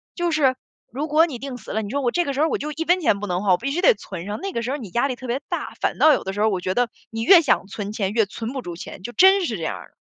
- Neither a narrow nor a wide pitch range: No, wide, 6.6 semitones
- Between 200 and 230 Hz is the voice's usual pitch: No, high, 245 Hz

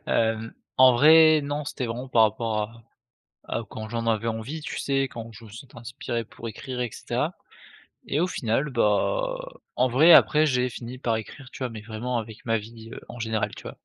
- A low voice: Yes, low, 120 Hz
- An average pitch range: Yes, average, 3.1 semitones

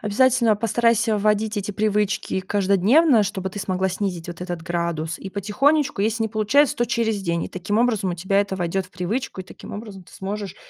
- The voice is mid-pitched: No, high, 205 Hz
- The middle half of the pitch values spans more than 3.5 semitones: No, average, 3.0 semitones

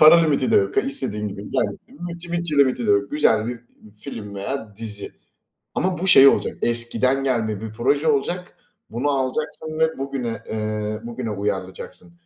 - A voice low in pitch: Yes, low, 125 Hz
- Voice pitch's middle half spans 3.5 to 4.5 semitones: No, wide, 5.4 semitones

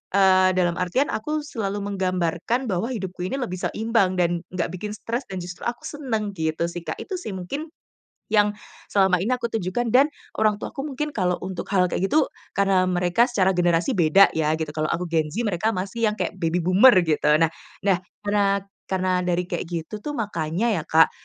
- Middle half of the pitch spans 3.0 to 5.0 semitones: Yes, average, 4.0 semitones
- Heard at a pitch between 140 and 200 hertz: Yes, high, 190 Hz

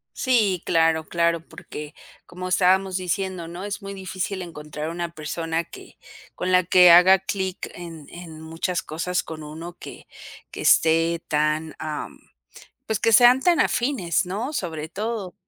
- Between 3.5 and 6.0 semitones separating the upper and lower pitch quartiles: No, average, 2.7 semitones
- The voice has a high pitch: No, medium, 175 Hz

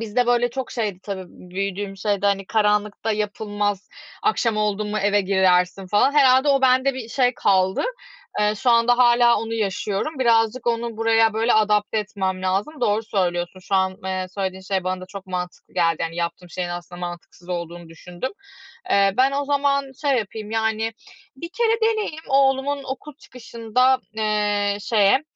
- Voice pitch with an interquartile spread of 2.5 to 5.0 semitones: Yes, average, 4.4 semitones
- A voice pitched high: Yes, high, 210 Hz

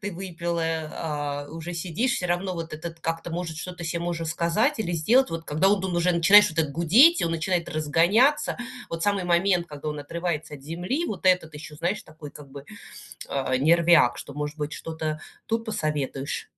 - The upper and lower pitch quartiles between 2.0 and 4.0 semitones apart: Yes, average, 2.7 semitones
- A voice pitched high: No, medium, 165 Hz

